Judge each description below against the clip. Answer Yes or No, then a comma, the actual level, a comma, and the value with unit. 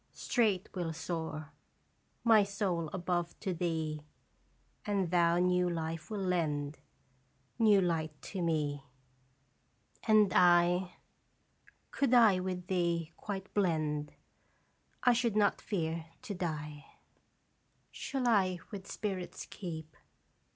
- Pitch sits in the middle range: Yes, medium, 180 Hz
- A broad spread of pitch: No, average, 3.7 semitones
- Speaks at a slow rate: Yes, slow, 110 wpm